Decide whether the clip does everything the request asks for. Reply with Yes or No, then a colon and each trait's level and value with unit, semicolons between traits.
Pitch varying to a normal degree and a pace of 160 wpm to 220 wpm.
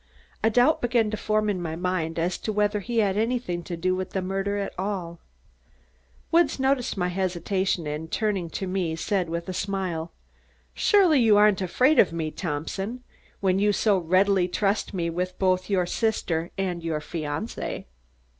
Yes: average, 3.5 semitones; average, 175 wpm